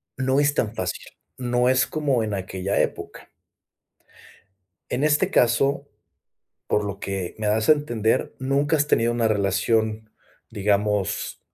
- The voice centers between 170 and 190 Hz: No, low, 115 Hz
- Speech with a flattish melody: No, average, 4.5 semitones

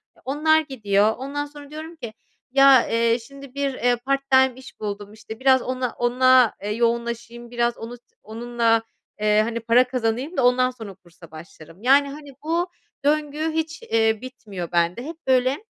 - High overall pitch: Yes, high, 245 Hz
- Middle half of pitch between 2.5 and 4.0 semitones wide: Yes, average, 3.5 semitones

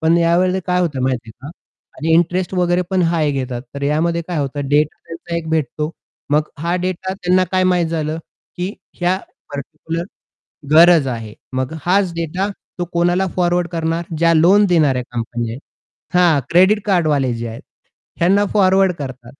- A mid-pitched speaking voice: Yes, medium, 165 Hz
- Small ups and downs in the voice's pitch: No, average, 3.7 semitones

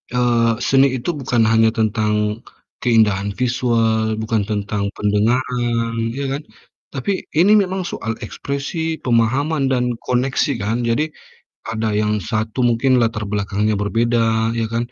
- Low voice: Yes, low, 115 Hz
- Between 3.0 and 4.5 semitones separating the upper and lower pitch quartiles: No, narrow, 2.5 semitones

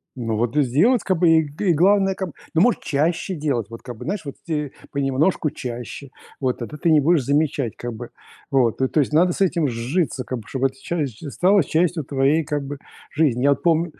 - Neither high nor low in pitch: Yes, medium, 145 Hz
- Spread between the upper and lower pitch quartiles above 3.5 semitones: Yes, average, 4.4 semitones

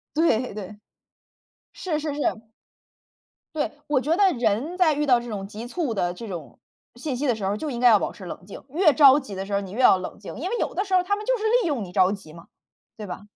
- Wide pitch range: Yes, wide, 7.5 semitones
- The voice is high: Yes, high, 245 Hz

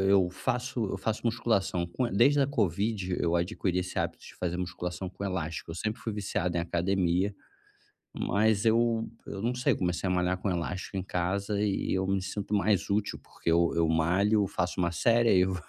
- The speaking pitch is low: Yes, very low, 95 Hz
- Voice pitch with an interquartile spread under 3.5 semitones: Yes, average, 3.1 semitones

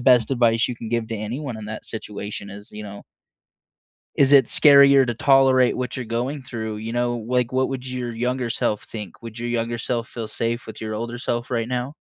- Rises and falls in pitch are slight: Yes, narrow, 2.2 semitones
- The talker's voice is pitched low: Yes, low, 120 Hz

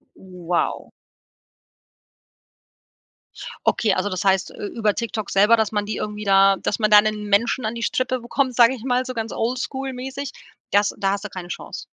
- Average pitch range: Yes, average, 3.6 semitones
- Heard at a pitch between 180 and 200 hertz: No, high, 215 Hz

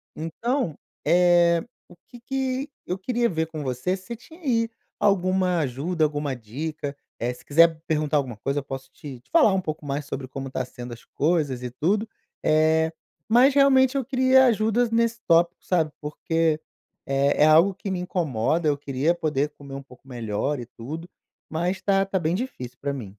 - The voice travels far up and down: Yes, wide, 5.7 semitones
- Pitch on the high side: No, medium, 160 Hz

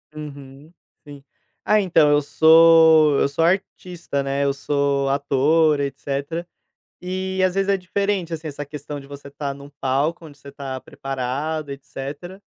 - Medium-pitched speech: Yes, medium, 145 Hz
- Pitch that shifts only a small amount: No, average, 3.0 semitones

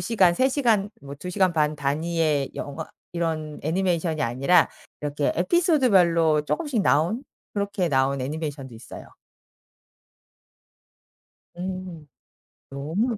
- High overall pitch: No, medium, 165 Hz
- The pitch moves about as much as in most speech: Yes, average, 4.6 semitones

